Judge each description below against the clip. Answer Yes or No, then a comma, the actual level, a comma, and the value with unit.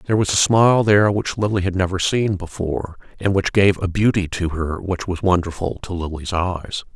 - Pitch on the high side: No, very low, 95 Hz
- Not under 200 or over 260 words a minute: Yes, fast, 205 wpm